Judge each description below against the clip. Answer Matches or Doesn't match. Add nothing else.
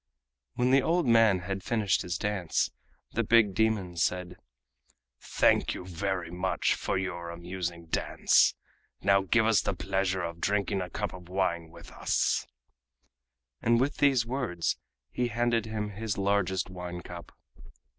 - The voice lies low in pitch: Matches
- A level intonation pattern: Doesn't match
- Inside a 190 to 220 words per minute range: Doesn't match